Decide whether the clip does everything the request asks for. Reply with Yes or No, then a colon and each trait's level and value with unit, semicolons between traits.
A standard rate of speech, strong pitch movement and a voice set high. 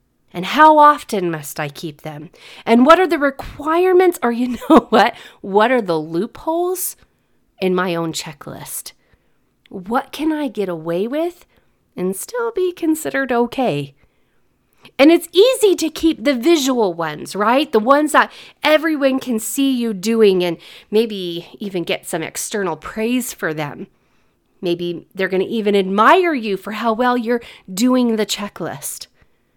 Yes: average, 150 wpm; wide, 8.0 semitones; high, 230 Hz